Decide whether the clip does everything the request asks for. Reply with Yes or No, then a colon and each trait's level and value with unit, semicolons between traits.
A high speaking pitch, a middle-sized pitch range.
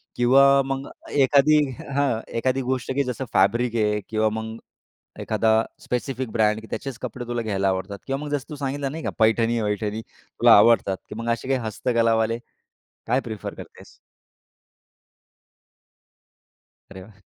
No: low, 115 Hz; average, 3.4 semitones